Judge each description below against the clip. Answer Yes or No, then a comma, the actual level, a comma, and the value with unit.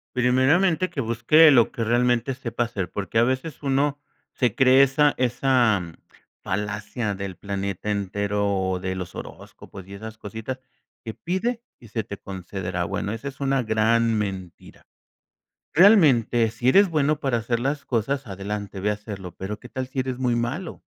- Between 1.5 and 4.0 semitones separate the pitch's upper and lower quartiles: No, average, 4.7 semitones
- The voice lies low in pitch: Yes, low, 115 Hz